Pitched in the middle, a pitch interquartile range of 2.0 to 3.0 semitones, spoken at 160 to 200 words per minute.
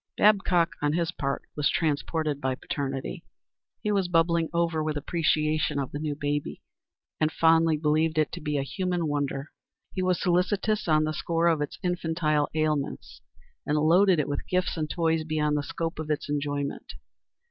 Yes: medium, 155 Hz; narrow, 2.5 semitones; average, 170 wpm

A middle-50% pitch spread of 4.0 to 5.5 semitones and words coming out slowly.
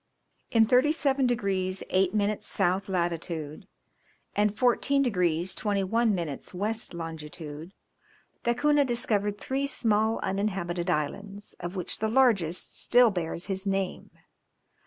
Yes: average, 4.5 semitones; slow, 115 wpm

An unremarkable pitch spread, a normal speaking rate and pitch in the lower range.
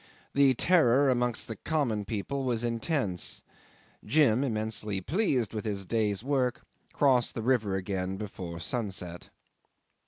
No: average, 4.6 semitones; slow, 125 wpm; low, 115 Hz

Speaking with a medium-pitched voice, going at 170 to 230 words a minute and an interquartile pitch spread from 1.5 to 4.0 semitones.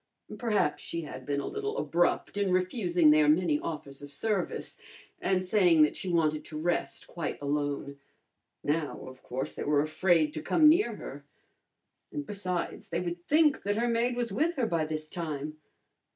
No: medium, 170 Hz; average, 175 wpm; average, 5.2 semitones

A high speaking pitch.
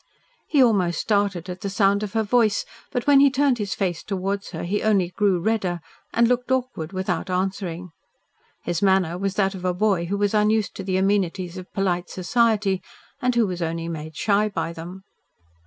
Yes: high, 195 Hz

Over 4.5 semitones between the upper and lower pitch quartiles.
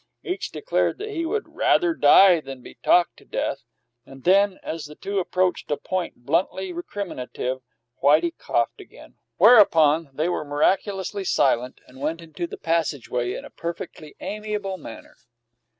Yes: average, 5.2 semitones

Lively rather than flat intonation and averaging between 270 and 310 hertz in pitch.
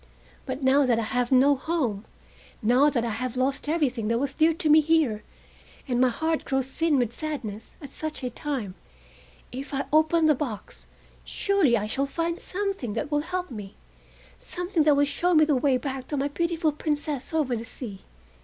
No: average, 4.1 semitones; very high, 280 Hz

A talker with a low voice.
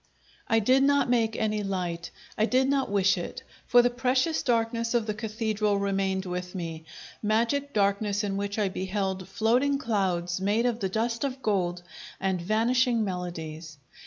No: high, 210 Hz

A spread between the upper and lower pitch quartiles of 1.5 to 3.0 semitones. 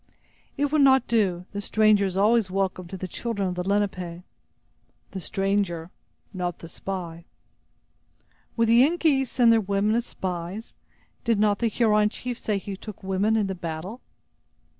No: average, 3.7 semitones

